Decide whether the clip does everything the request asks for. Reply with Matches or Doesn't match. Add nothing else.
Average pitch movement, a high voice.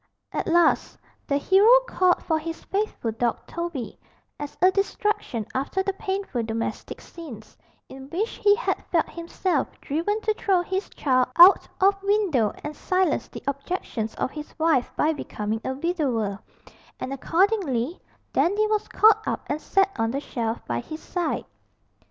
Doesn't match